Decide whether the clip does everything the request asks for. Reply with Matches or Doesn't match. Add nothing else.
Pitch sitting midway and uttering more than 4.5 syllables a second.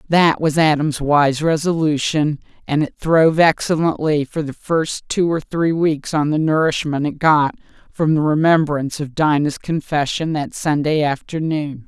Doesn't match